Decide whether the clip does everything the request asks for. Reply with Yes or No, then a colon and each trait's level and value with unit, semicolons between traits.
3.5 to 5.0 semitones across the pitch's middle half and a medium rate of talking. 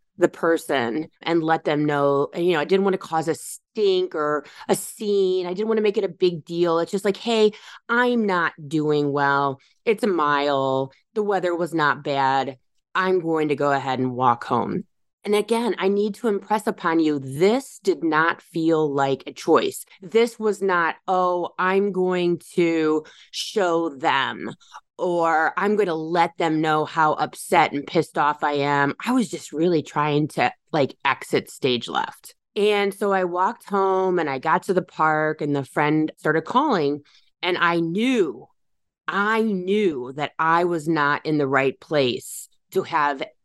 Yes: average, 4.6 semitones; average, 180 wpm